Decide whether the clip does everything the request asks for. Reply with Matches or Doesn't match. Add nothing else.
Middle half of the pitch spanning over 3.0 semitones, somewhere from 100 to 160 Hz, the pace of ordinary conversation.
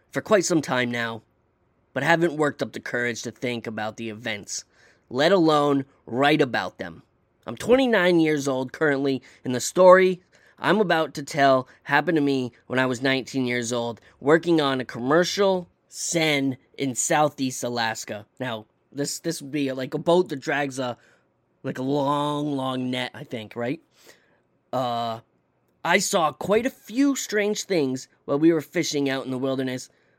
Matches